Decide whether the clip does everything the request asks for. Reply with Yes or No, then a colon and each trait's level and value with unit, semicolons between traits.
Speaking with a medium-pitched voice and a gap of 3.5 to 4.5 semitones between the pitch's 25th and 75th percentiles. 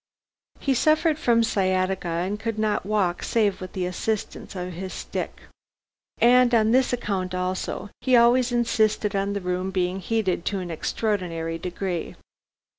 No: high, 200 Hz; average, 3.8 semitones